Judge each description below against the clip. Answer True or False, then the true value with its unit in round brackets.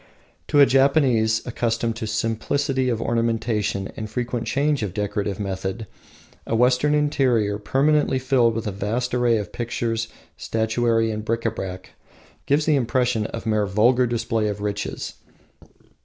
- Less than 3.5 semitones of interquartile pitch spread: True (2.9 semitones)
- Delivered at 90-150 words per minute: True (145 wpm)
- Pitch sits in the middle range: False (115 Hz)